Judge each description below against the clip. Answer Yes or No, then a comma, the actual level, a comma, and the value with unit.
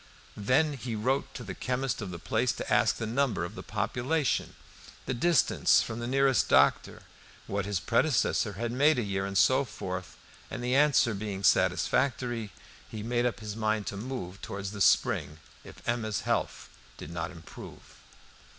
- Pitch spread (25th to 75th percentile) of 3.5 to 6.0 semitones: Yes, average, 4.3 semitones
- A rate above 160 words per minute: Yes, average, 170 wpm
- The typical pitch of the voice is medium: No, low, 115 Hz